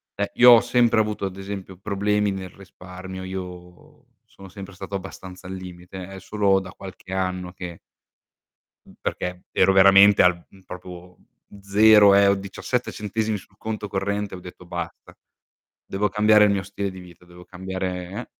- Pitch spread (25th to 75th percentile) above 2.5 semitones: No, narrow, 1.8 semitones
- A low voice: Yes, very low, 95 Hz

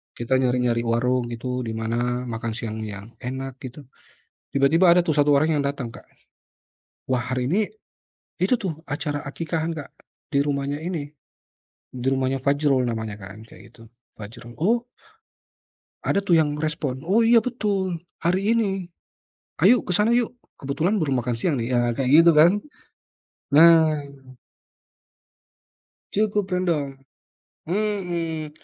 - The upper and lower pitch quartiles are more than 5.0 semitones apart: Yes, wide, 5.6 semitones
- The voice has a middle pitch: Yes, medium, 145 Hz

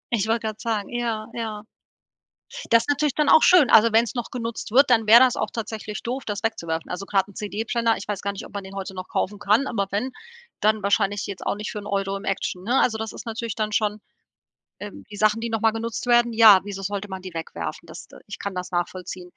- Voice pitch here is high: Yes, high, 215 Hz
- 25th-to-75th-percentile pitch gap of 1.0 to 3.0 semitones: Yes, average, 2.7 semitones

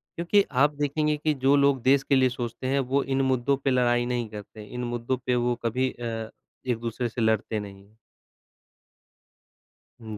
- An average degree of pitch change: Yes, average, 3.1 semitones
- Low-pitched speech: Yes, low, 125 Hz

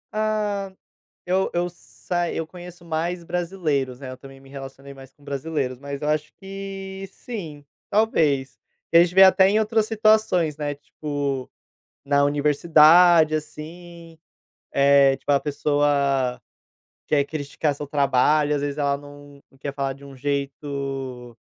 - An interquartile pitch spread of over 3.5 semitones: Yes, average, 3.9 semitones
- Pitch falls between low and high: Yes, medium, 150 Hz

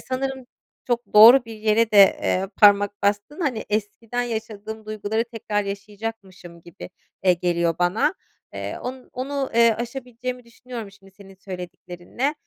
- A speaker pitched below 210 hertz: No, high, 220 Hz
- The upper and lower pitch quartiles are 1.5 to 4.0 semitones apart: Yes, average, 3.5 semitones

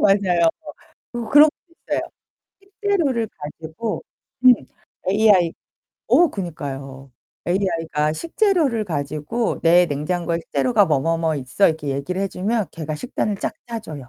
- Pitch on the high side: No, medium, 180 Hz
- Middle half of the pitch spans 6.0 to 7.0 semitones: Yes, wide, 6.7 semitones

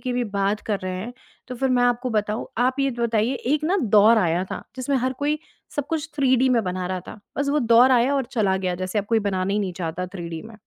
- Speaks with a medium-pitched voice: No, high, 225 Hz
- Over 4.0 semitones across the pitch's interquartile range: Yes, average, 5.3 semitones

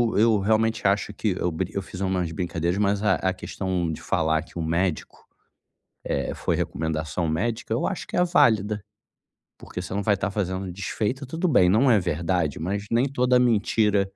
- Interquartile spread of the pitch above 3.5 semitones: Yes, average, 3.9 semitones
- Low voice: Yes, low, 100 Hz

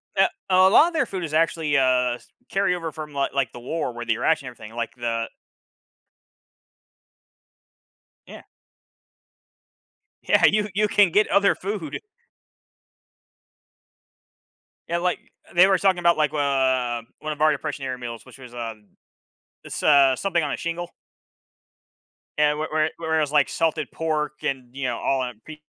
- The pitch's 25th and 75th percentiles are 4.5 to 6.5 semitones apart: Yes, average, 5.0 semitones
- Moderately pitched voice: Yes, medium, 150 Hz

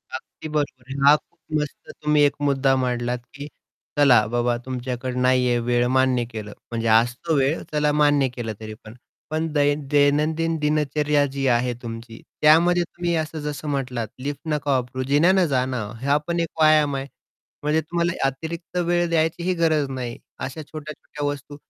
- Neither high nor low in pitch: Yes, medium, 145 Hz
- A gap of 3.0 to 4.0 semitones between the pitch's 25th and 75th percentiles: Yes, average, 3.5 semitones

